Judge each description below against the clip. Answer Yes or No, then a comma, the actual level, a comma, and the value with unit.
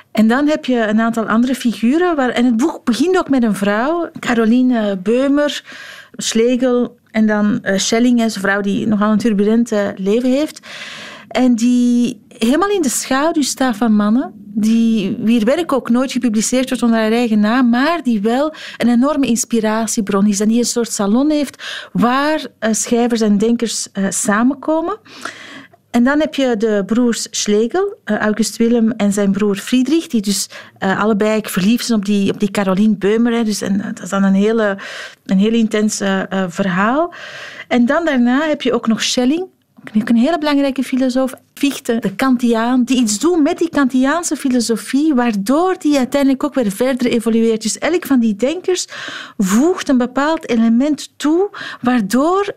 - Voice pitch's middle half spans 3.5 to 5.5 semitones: Yes, average, 3.9 semitones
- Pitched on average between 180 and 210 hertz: No, high, 240 Hz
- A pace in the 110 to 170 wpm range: Yes, average, 160 wpm